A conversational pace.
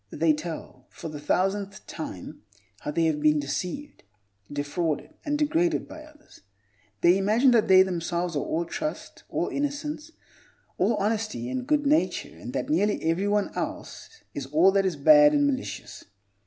Yes: average, 155 wpm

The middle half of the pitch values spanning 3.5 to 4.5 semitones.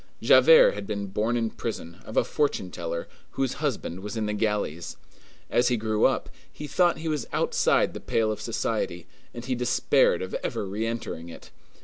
Yes: average, 3.8 semitones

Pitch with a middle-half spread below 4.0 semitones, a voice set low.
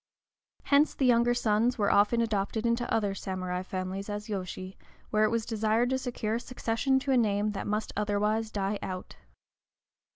No: average, 2.7 semitones; high, 215 Hz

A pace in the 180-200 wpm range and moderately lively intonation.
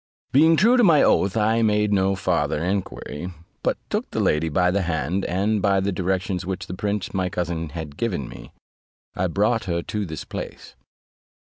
Yes: average, 185 wpm; average, 3.4 semitones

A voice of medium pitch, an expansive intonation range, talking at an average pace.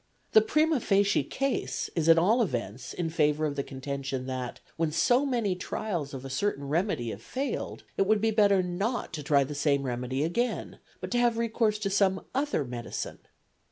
Yes: medium, 175 Hz; wide, 7.8 semitones; average, 190 wpm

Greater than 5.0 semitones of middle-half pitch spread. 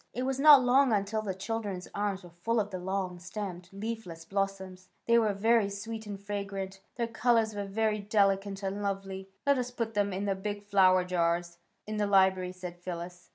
No: narrow, 2.6 semitones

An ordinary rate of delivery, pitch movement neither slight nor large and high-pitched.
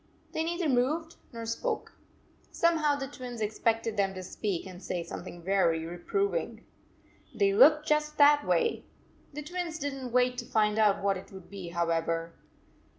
No: average, 170 wpm; wide, 8.0 semitones; high, 245 Hz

